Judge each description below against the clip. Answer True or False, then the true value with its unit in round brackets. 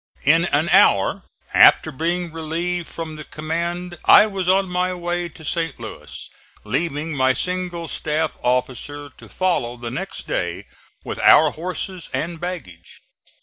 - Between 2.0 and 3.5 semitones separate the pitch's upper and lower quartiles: True (2.9 semitones)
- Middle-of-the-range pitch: True (165 Hz)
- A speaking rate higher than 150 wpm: False (145 wpm)